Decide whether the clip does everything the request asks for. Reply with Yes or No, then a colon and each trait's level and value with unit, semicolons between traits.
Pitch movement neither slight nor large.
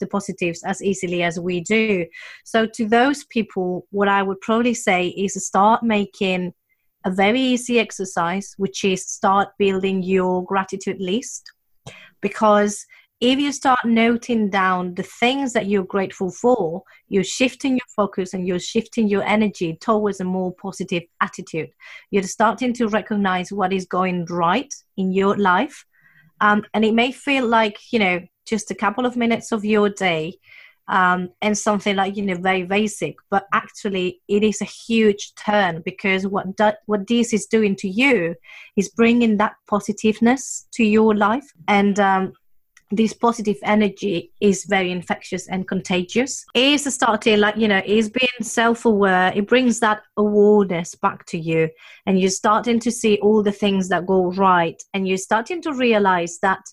Yes: average, 3.0 semitones